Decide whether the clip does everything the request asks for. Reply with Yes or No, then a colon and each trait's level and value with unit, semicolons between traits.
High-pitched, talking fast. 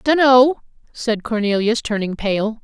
No: high, 230 Hz; slow, 115 wpm